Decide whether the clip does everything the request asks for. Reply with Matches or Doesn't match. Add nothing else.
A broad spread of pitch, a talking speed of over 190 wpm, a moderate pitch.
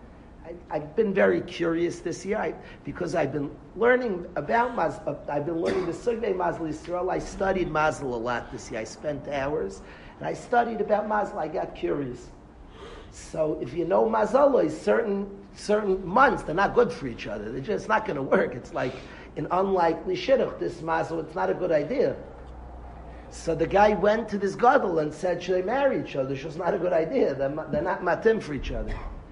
Matches